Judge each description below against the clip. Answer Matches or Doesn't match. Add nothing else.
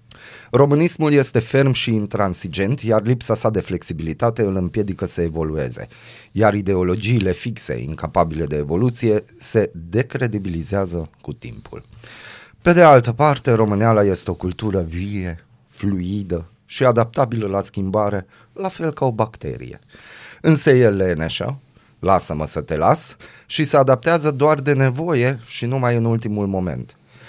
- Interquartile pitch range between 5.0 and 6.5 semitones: Matches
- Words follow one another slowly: Doesn't match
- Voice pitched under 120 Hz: Matches